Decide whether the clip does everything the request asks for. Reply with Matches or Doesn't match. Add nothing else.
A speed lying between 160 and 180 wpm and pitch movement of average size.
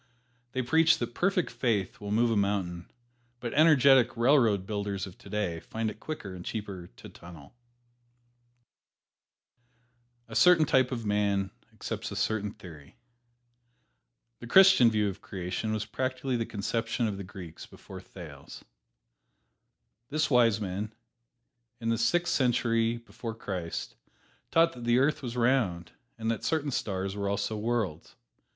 Doesn't match